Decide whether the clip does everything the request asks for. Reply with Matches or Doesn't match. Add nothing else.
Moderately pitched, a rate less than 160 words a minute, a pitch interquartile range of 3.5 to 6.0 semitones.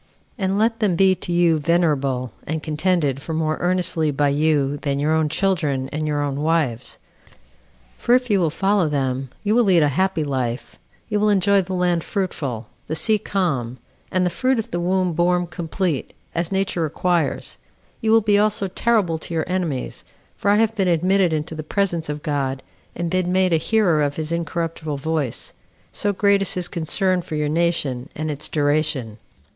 Doesn't match